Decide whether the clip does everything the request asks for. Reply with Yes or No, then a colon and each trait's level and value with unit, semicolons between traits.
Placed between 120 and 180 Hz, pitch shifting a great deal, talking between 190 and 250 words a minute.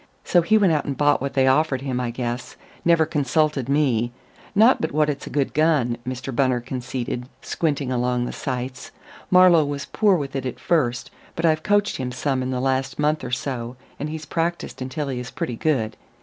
No: low, 135 Hz; average, 3.7 semitones; fast, 205 wpm